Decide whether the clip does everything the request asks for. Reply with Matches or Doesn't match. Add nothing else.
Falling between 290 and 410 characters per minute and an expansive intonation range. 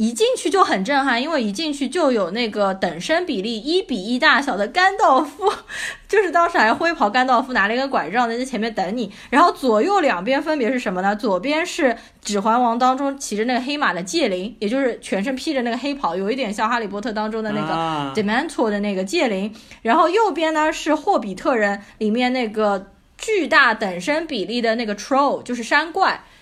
Matches